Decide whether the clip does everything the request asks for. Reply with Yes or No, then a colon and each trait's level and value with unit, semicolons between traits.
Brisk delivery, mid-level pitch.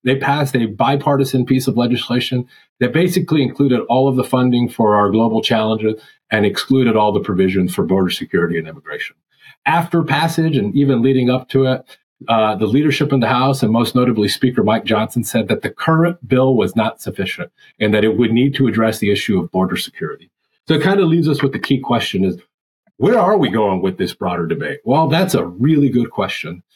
No: fast, 210 wpm; low, 125 Hz